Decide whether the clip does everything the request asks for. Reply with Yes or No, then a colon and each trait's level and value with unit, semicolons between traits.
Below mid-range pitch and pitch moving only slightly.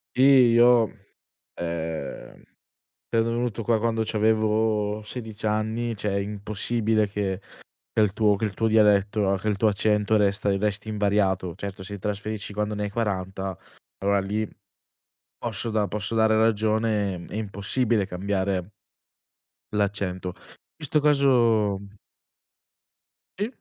Yes: low, 105 Hz; narrow, 1.9 semitones